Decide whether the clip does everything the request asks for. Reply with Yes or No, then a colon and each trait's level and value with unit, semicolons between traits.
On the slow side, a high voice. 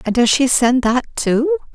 No: fast, 205 wpm; high, 235 Hz